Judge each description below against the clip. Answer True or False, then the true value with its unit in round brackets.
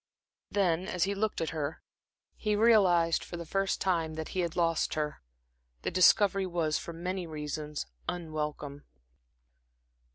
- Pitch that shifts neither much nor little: True (3.2 semitones)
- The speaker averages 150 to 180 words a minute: False (140 wpm)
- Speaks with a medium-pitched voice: True (170 Hz)